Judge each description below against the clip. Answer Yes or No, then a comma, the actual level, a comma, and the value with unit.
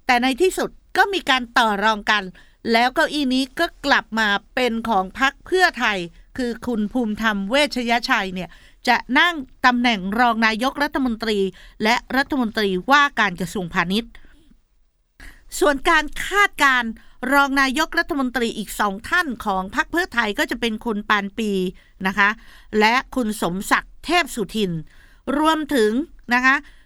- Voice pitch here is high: Yes, high, 245 Hz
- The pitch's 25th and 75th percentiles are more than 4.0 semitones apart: Yes, average, 4.7 semitones